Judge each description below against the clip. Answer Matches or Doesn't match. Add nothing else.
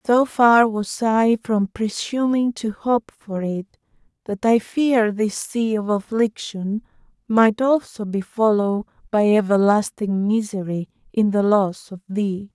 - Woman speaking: Matches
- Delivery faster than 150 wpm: Doesn't match